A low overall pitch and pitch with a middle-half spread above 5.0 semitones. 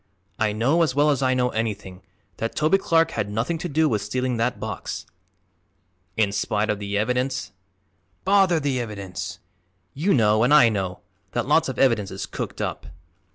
Yes: low, 120 Hz; wide, 5.6 semitones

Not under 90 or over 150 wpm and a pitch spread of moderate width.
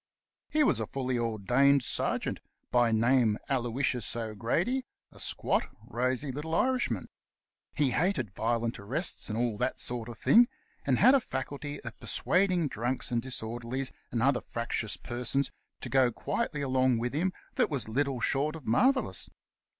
No: average, 160 wpm; average, 3.8 semitones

